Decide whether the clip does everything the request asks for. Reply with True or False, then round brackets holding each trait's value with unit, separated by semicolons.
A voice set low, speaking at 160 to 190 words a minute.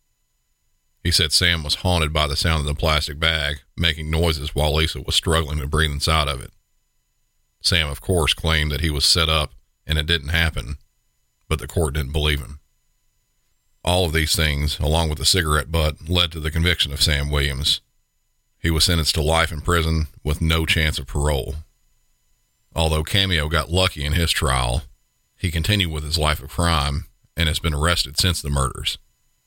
True (80 Hz; 185 wpm)